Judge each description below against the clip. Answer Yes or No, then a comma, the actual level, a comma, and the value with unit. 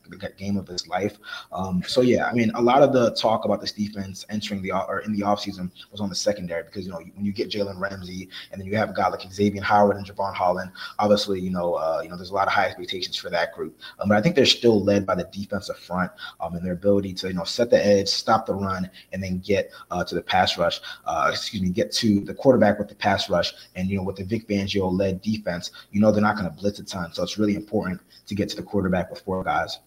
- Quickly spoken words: Yes, fast, 275 wpm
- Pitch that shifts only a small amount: Yes, narrow, 1.5 semitones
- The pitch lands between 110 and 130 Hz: No, low, 100 Hz